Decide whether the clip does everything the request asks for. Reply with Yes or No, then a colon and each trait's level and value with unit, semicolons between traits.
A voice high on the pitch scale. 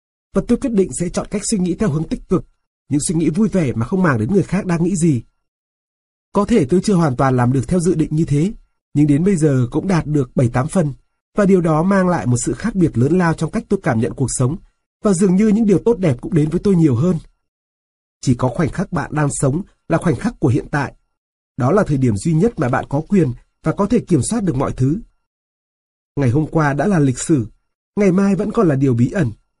No: medium, 160 Hz